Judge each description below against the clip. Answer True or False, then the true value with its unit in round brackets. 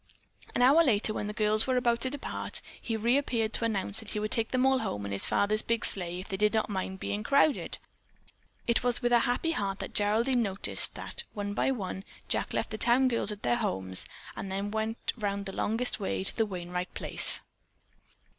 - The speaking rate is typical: False (210 wpm)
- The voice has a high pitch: True (215 Hz)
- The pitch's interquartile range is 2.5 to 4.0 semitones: True (3.4 semitones)